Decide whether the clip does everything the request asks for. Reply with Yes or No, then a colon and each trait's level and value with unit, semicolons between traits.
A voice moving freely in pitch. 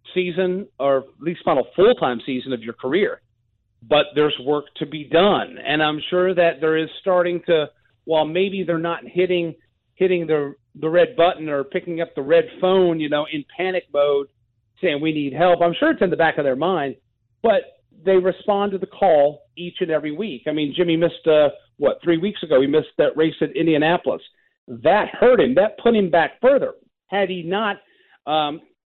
No: average, 3.7 semitones